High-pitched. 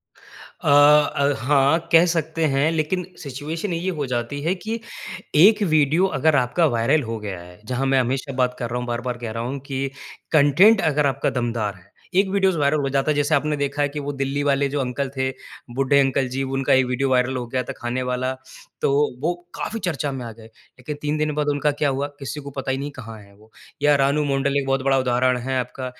No: low, 135 Hz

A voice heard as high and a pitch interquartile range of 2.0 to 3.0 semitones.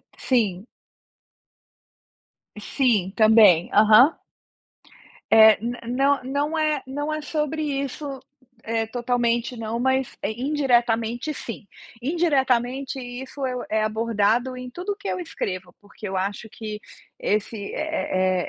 No: high, 245 Hz; average, 4.3 semitones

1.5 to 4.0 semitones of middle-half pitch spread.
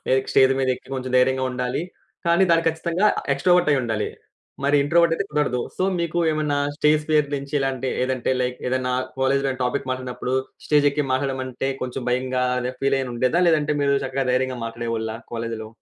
Yes: average, 2.9 semitones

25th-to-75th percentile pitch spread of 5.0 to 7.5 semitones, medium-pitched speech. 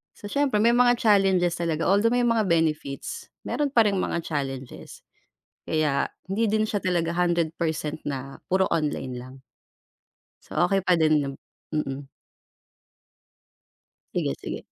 Yes: average, 5.3 semitones; medium, 170 Hz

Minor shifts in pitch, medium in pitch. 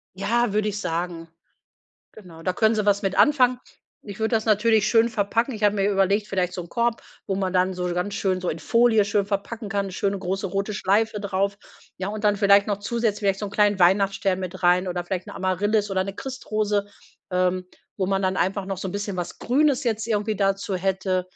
No: narrow, 2.3 semitones; high, 200 Hz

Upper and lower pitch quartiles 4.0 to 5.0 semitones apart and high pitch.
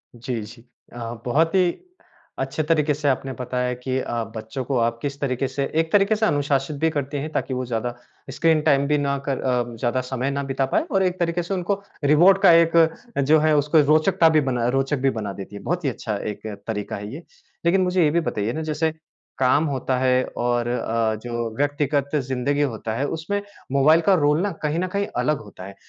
No: average, 4.4 semitones; medium, 140 Hz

